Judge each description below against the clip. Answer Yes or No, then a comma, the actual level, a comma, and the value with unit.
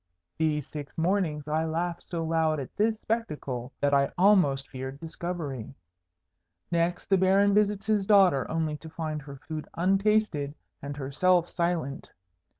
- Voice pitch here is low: No, medium, 160 Hz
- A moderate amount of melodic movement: Yes, average, 4.6 semitones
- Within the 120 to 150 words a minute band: Yes, average, 145 wpm